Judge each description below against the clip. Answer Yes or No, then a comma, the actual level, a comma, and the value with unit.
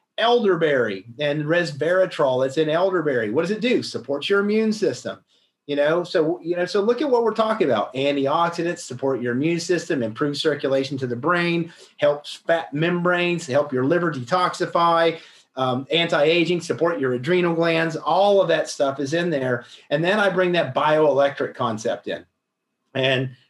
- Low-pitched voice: No, medium, 165 Hz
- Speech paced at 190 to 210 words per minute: No, average, 165 wpm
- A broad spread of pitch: No, average, 3.9 semitones